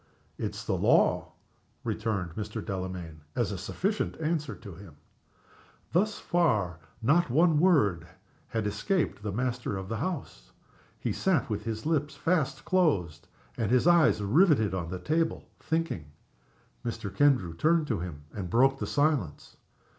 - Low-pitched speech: Yes, low, 115 Hz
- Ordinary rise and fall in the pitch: No, wide, 8.8 semitones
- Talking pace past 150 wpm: No, average, 145 wpm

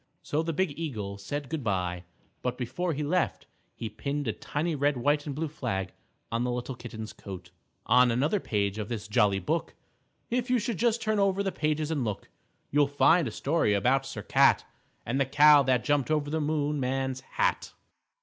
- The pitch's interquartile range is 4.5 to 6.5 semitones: Yes, average, 5.1 semitones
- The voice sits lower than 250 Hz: Yes, medium, 140 Hz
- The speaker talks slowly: No, average, 190 wpm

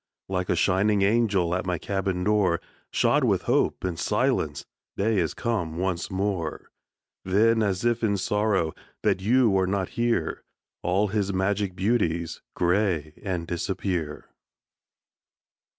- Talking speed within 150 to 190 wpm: No, slow, 135 wpm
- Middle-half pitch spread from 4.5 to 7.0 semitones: No, average, 2.8 semitones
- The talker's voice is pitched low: Yes, very low, 95 Hz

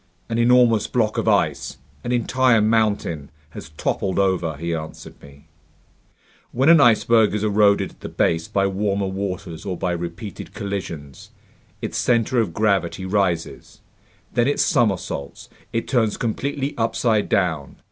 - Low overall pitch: Yes, low, 100 Hz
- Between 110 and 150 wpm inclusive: Yes, average, 140 wpm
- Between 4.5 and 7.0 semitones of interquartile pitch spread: Yes, average, 4.8 semitones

